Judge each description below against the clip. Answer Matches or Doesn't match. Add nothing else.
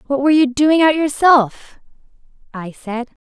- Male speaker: Doesn't match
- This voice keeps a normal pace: Matches